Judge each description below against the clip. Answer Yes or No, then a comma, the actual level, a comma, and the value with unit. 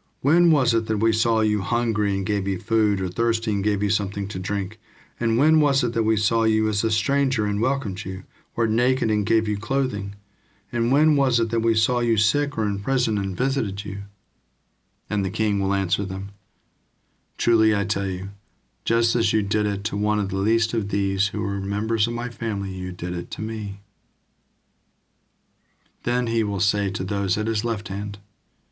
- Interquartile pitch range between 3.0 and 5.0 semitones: No, narrow, 2.5 semitones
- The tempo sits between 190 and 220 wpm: Yes, fast, 205 wpm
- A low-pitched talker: Yes, low, 105 Hz